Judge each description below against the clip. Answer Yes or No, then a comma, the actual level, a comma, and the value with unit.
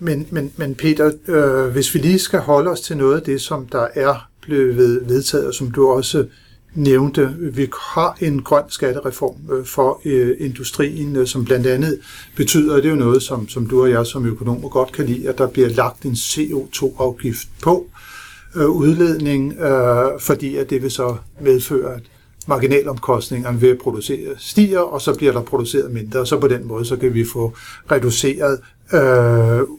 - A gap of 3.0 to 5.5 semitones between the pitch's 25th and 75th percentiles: No, narrow, 2.6 semitones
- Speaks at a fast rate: No, average, 180 wpm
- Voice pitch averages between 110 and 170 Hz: Yes, low, 135 Hz